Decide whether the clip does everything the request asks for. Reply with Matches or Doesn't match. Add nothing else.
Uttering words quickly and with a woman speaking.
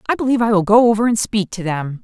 Matches